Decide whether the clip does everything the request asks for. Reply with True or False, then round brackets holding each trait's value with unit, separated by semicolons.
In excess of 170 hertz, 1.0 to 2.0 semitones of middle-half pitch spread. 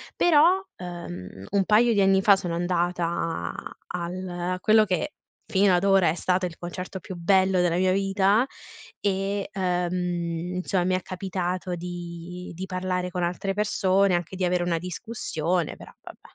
True (185 Hz; 1.7 semitones)